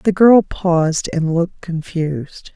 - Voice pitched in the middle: Yes, medium, 170 Hz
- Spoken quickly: No, average, 140 wpm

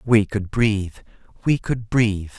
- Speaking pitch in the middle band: No, low, 110 Hz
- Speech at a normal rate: Yes, average, 150 wpm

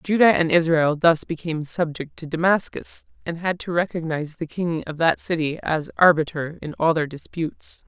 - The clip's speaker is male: No, female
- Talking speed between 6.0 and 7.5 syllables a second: No, 5.0 syllables/s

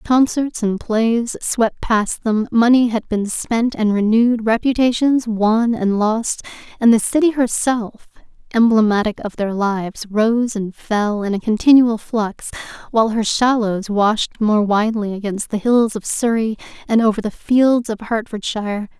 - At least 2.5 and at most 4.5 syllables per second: Yes, 4.3 syllables/s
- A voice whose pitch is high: Yes, high, 225 Hz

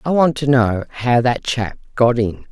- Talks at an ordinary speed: No, fast, 215 wpm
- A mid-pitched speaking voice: No, low, 125 Hz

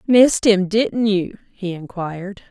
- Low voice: No, high, 200 Hz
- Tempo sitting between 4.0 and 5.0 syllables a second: Yes, 4.2 syllables/s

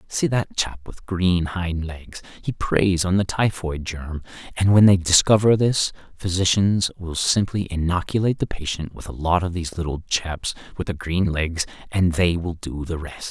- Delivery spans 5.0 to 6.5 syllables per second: No, 4.6 syllables/s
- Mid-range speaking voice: No, very low, 90 Hz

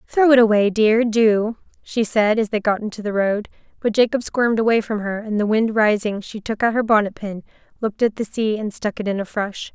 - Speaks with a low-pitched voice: No, high, 215 Hz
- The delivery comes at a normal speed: No, fast, 235 wpm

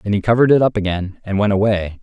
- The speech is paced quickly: Yes, fast, 265 wpm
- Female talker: No, male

